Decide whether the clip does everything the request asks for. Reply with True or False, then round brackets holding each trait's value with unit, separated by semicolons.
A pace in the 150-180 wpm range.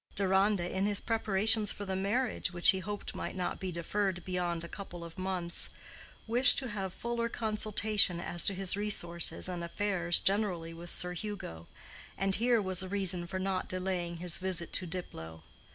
True (175 wpm)